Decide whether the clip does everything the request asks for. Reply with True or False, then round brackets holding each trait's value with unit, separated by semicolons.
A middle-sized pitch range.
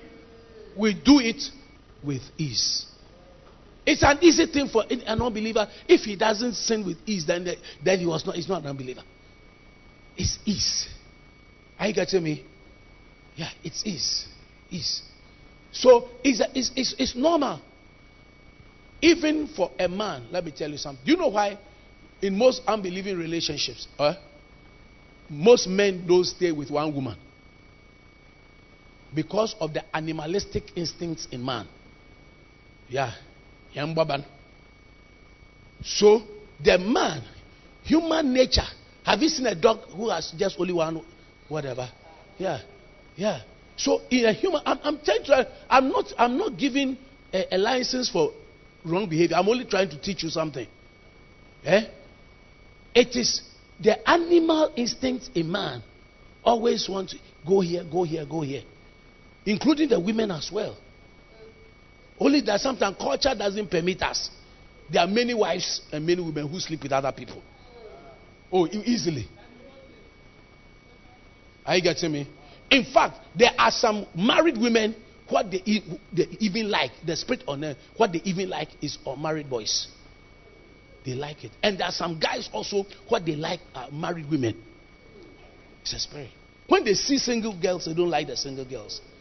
False (7.4 semitones)